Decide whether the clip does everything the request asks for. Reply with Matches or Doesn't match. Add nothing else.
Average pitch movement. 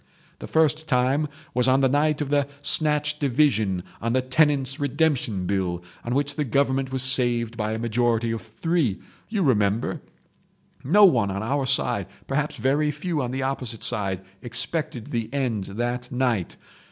Matches